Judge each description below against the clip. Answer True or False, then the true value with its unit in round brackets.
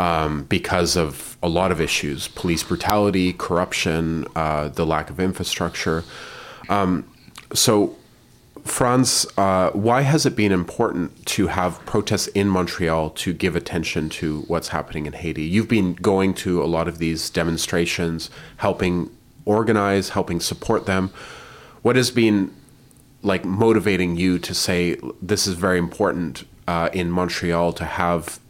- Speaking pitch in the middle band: False (90 Hz)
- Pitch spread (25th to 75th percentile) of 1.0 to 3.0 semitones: False (3.6 semitones)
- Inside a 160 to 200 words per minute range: False (145 wpm)